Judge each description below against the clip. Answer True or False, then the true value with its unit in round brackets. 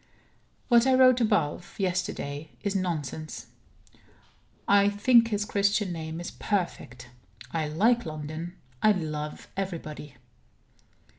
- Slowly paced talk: True (115 wpm)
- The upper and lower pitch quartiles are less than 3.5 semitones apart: False (4.9 semitones)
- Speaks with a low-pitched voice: False (180 Hz)